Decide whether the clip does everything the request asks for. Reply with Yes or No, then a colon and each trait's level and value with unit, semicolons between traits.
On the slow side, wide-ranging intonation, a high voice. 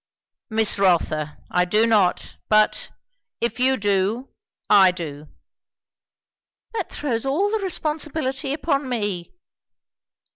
Yes: slow, 105 wpm; wide, 6.5 semitones; high, 225 Hz